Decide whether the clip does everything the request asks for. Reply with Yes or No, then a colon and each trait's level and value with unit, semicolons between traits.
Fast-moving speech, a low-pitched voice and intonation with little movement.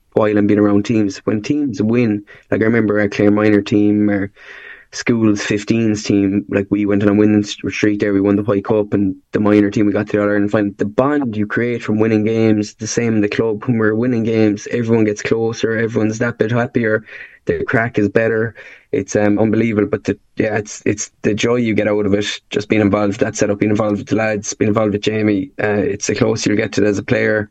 Yes: fast, 240 wpm; low, 105 Hz; narrow, 1.4 semitones